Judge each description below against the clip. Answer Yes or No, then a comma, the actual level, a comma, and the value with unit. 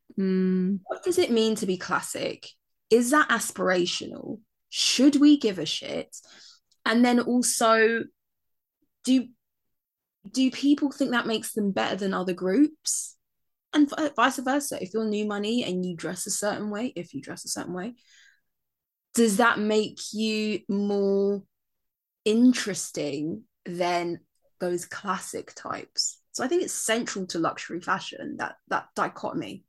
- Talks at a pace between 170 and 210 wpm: No, average, 140 wpm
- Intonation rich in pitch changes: No, average, 4.8 semitones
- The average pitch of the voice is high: Yes, high, 220 Hz